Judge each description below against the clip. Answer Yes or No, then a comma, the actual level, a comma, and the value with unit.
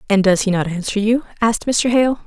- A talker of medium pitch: No, high, 215 Hz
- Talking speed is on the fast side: Yes, fast, 240 wpm